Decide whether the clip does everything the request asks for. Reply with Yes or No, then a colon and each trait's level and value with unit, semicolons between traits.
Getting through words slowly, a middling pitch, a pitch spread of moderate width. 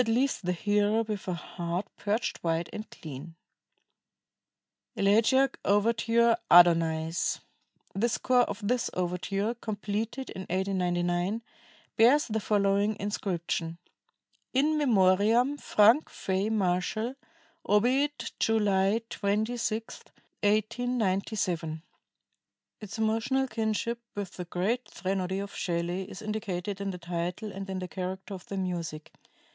No: slow, 110 wpm; high, 205 Hz; average, 3.7 semitones